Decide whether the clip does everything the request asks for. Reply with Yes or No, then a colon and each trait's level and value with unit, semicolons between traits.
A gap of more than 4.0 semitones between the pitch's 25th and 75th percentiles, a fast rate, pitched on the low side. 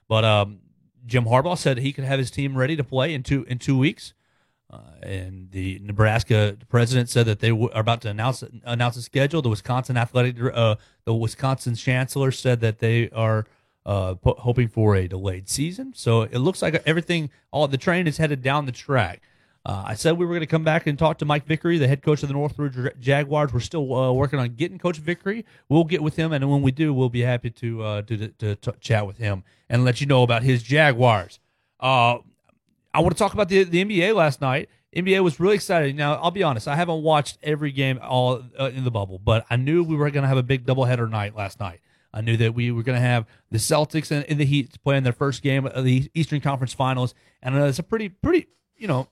Yes: average, 4.4 semitones; fast, 240 wpm; low, 130 Hz